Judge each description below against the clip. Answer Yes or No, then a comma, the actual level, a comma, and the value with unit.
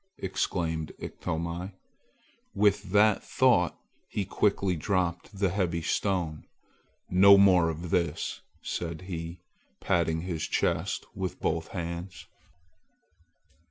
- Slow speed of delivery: Yes, slow, 100 wpm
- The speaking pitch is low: Yes, very low, 90 Hz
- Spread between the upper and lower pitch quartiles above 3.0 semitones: No, average, 2.7 semitones